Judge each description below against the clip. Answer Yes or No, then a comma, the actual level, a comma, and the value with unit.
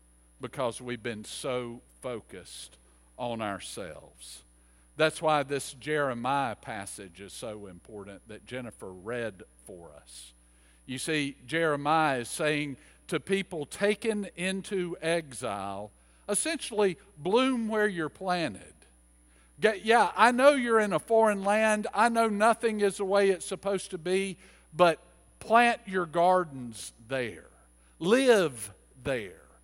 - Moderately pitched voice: Yes, medium, 150 Hz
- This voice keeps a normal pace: No, slow, 125 wpm